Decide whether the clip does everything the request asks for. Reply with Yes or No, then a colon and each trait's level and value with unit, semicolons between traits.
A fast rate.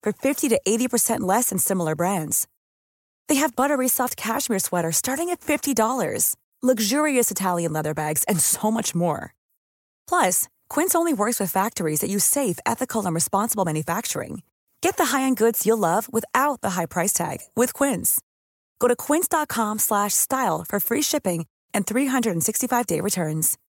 No: average, 155 wpm